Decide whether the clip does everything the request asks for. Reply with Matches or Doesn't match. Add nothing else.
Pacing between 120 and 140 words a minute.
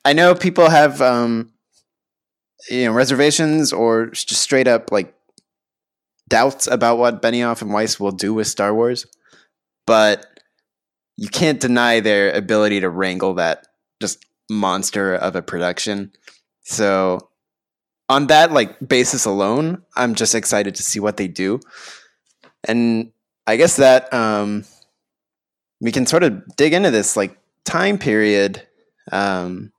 Matches